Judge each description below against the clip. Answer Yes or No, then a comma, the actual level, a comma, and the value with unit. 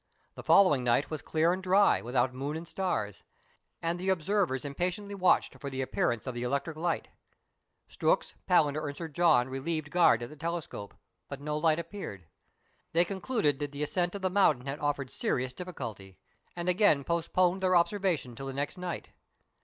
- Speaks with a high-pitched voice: No, medium, 155 Hz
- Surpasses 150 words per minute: Yes, average, 180 wpm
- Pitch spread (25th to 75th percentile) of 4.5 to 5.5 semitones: Yes, average, 4.9 semitones